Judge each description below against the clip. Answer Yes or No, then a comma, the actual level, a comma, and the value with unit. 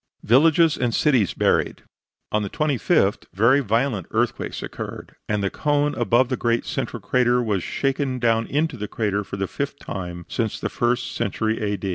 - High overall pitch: No, low, 120 Hz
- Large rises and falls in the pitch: No, average, 4.6 semitones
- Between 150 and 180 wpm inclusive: Yes, average, 170 wpm